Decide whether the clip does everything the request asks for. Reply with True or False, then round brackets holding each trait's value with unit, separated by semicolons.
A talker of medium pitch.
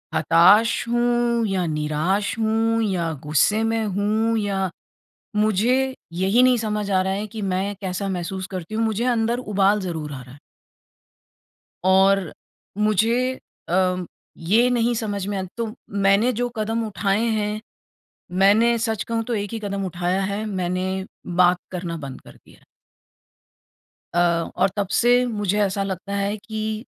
False (205 Hz)